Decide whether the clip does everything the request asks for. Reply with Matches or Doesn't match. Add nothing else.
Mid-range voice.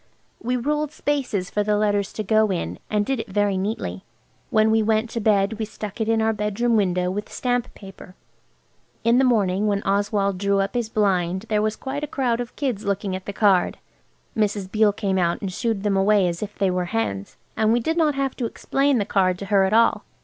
Doesn't match